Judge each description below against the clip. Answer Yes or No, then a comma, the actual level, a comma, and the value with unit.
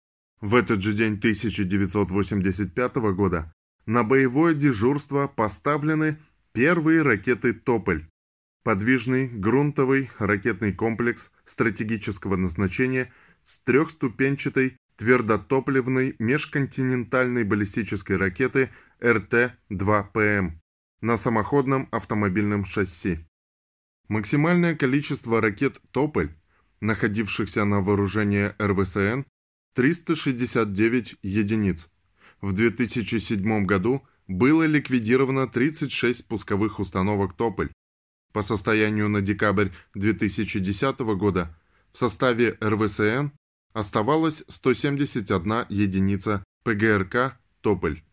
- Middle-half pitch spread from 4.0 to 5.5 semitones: Yes, average, 4.3 semitones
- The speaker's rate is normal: No, slow, 80 wpm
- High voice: No, low, 110 Hz